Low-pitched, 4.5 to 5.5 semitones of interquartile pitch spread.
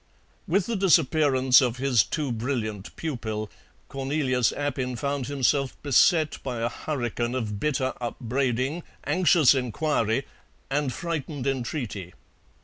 No: low, 130 Hz; average, 3.6 semitones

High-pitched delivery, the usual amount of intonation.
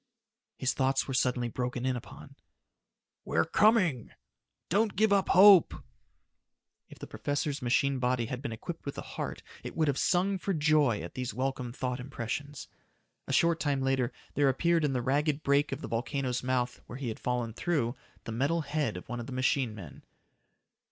No: low, 135 Hz; average, 3.6 semitones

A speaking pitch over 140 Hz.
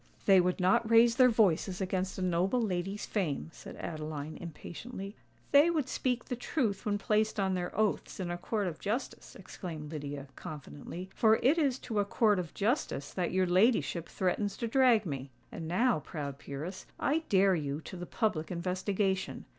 Yes: high, 190 Hz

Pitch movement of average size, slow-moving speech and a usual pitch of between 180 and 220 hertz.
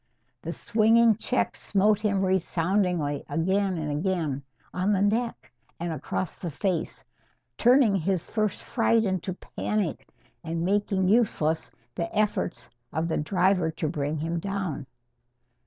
Yes: average, 4.1 semitones; slow, 130 wpm; medium, 185 Hz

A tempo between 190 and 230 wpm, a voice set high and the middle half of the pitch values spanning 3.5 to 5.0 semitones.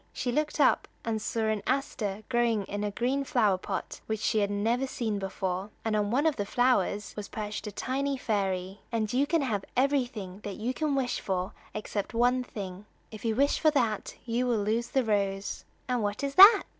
Yes: average, 200 wpm; high, 220 Hz; average, 3.8 semitones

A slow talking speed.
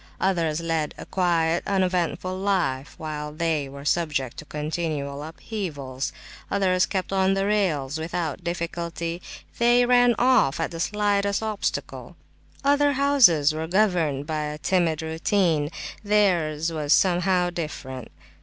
Yes: slow, 125 wpm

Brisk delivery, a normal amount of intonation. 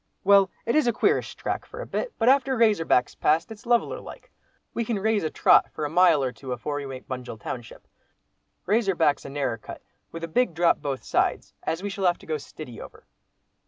No: fast, 225 wpm; wide, 7.7 semitones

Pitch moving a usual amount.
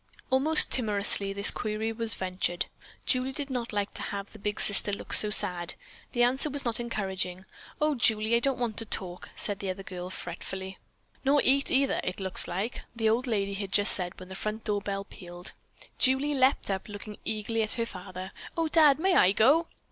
Yes: average, 4.7 semitones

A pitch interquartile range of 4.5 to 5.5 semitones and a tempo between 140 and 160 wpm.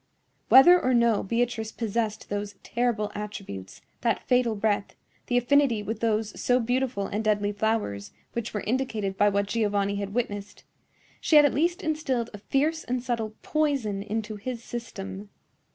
No: average, 3.2 semitones; average, 155 wpm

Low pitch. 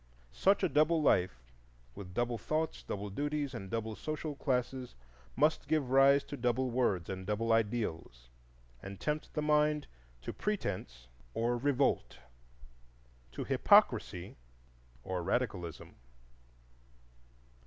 Yes: low, 125 Hz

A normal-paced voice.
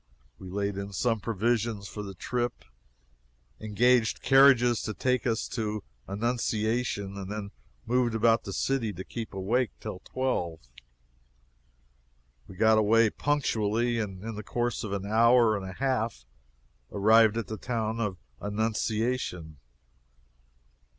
No: slow, 130 wpm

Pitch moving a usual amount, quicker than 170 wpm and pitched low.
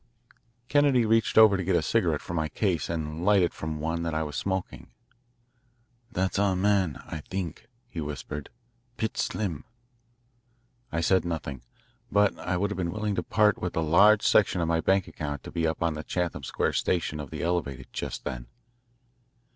Yes: average, 4.1 semitones; average, 180 wpm; very low, 85 Hz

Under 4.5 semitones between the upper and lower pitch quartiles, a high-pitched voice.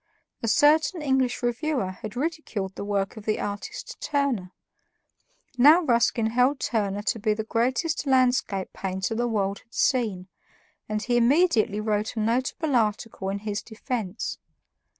Yes: average, 4.0 semitones; high, 230 Hz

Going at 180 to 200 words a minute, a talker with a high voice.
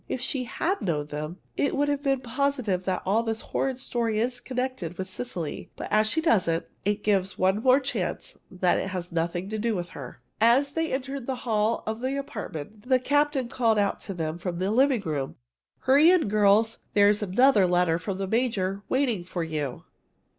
Yes: average, 195 wpm; high, 215 Hz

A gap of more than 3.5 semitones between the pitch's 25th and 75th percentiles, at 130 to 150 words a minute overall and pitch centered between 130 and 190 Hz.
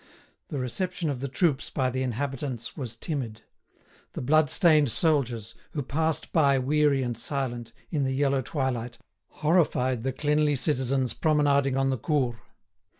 No: average, 3.0 semitones; average, 145 wpm; low, 135 Hz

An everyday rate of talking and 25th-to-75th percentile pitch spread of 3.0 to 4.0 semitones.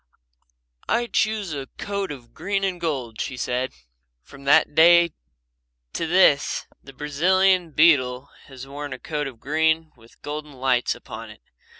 No: average, 150 wpm; average, 4.4 semitones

